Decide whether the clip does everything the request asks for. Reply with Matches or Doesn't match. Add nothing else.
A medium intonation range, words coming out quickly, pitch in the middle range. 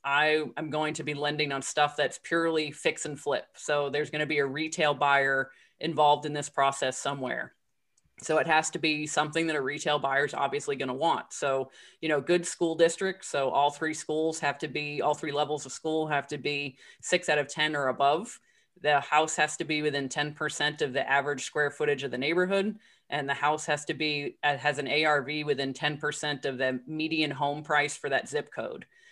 Doesn't match